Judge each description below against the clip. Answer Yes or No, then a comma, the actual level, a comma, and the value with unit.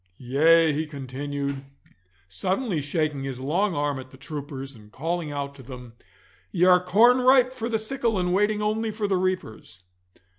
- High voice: No, medium, 160 Hz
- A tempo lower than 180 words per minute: Yes, average, 170 wpm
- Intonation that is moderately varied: No, wide, 7.0 semitones